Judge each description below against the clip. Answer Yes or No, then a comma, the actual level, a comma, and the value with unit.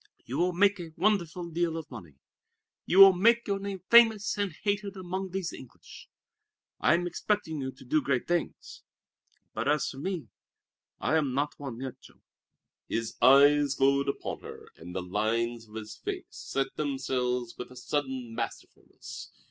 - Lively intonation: Yes, wide, 6.4 semitones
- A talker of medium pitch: Yes, medium, 145 Hz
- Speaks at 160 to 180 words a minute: Yes, average, 165 wpm